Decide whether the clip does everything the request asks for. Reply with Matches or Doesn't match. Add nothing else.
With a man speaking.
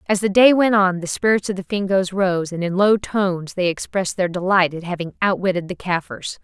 Doesn't match